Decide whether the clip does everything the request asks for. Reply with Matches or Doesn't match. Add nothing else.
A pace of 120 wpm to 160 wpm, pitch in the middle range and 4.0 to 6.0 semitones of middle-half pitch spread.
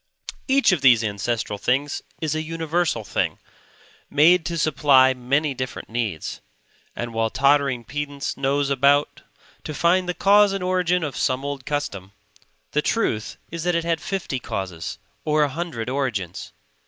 Matches